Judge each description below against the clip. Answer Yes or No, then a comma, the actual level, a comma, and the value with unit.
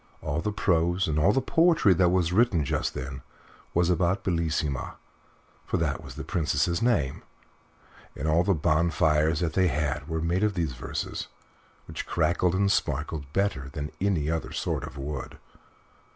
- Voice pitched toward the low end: Yes, very low, 85 Hz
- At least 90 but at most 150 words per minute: No, average, 160 wpm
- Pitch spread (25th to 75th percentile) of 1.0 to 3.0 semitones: No, average, 3.6 semitones